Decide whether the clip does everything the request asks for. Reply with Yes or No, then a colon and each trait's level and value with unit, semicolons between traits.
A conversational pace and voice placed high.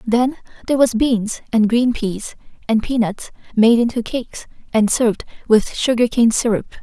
Yes: average, 150 wpm; high, 230 Hz